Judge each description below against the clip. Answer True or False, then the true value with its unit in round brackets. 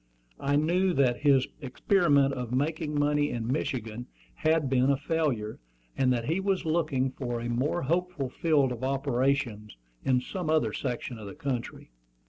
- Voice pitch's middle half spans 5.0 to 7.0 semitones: False (3.9 semitones)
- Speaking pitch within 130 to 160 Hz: True (135 Hz)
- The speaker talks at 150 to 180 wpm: True (160 wpm)